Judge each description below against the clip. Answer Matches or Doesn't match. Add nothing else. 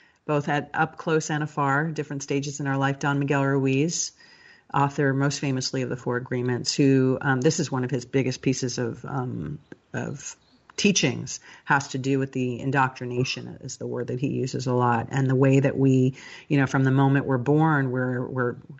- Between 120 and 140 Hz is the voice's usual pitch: Matches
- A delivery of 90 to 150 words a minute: Doesn't match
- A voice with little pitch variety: Matches